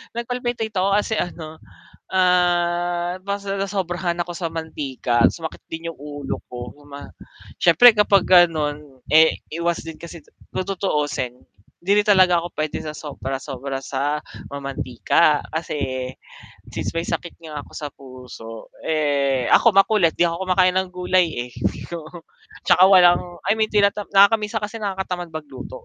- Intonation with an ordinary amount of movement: Yes, average, 4.4 semitones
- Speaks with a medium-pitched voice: Yes, medium, 170 Hz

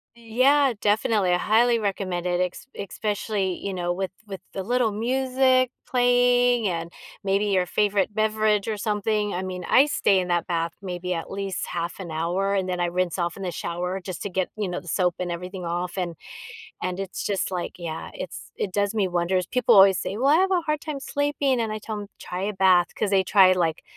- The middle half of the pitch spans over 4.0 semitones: No, average, 3.5 semitones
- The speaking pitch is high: Yes, high, 195 Hz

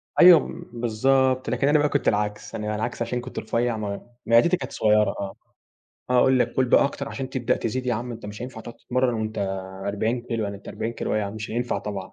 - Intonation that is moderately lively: Yes, average, 3.2 semitones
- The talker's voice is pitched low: Yes, low, 120 Hz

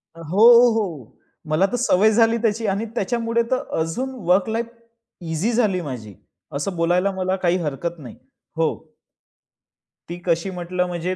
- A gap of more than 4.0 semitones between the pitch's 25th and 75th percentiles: Yes, average, 4.7 semitones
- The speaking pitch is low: No, medium, 185 Hz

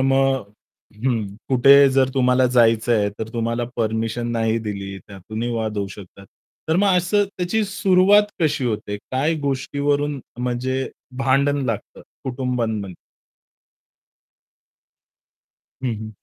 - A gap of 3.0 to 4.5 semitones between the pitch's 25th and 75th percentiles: Yes, average, 3.9 semitones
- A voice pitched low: Yes, low, 125 Hz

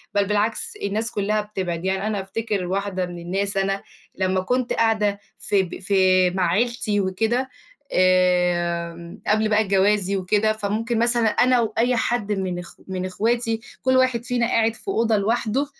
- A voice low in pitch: No, high, 205 Hz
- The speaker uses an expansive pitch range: No, average, 3.3 semitones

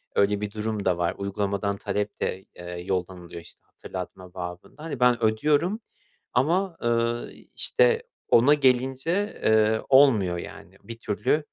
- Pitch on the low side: Yes, low, 110 Hz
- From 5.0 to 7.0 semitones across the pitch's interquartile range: Yes, wide, 5.6 semitones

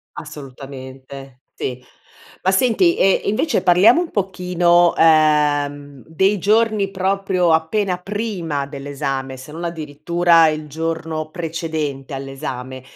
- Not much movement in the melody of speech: No, average, 4.8 semitones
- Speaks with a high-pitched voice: No, medium, 160 Hz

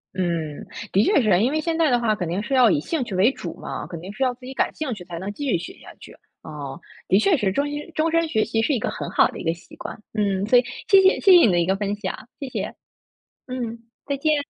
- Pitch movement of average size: No, wide, 7.0 semitones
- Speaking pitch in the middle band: No, high, 225 Hz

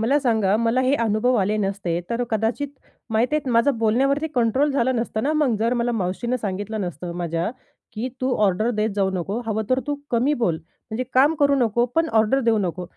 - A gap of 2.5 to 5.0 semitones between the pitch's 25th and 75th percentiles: Yes, average, 3.8 semitones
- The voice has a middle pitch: No, high, 230 Hz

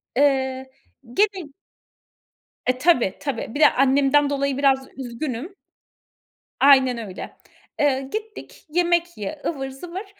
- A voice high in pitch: Yes, very high, 275 Hz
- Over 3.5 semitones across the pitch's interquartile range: Yes, average, 4.0 semitones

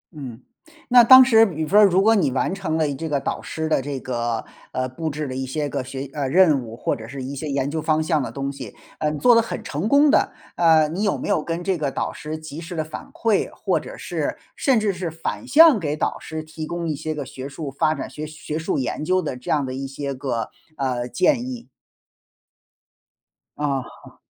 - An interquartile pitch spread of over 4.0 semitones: Yes, average, 4.6 semitones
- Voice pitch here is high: No, medium, 155 Hz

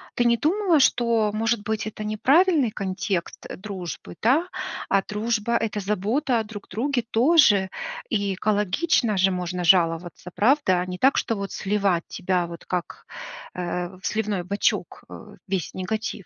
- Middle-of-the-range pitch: No, high, 210 Hz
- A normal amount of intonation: Yes, average, 4.1 semitones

